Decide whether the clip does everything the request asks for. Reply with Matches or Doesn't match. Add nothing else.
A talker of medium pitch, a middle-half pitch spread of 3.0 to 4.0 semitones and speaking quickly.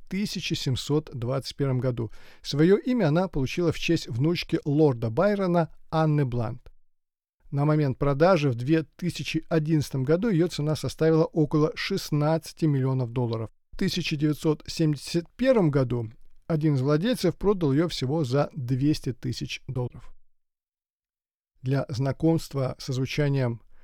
Doesn't match